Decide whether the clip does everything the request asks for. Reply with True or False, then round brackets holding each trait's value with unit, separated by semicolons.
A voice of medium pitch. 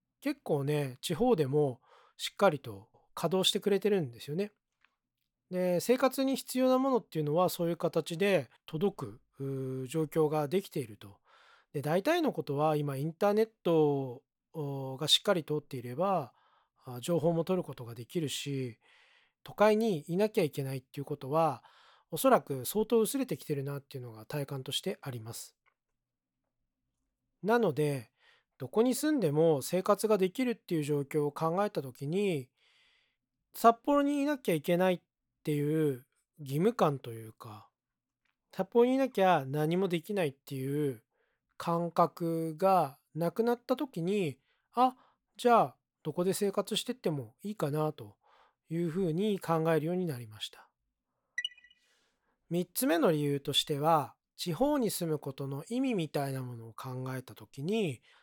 True (165 Hz)